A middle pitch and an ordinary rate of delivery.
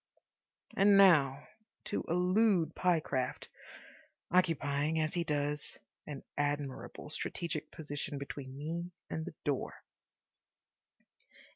No: medium, 155 Hz; slow, 95 wpm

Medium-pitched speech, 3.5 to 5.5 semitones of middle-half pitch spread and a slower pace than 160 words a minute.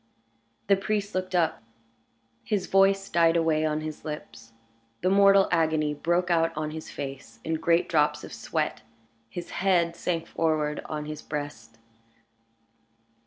No: medium, 165 Hz; average, 3.1 semitones; average, 140 wpm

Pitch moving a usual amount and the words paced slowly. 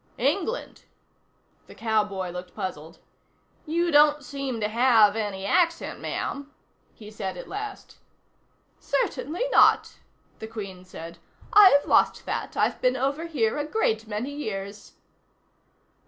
No: wide, 6.5 semitones; slow, 125 wpm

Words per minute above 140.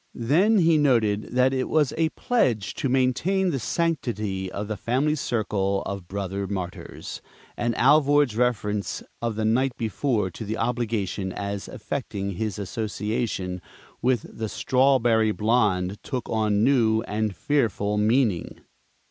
No: slow, 135 wpm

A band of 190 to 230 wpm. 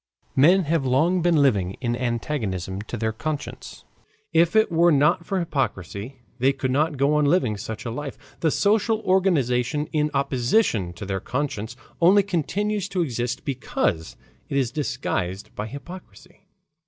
No: average, 155 wpm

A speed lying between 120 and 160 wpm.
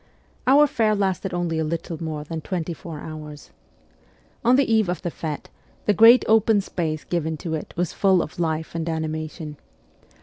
No: average, 175 wpm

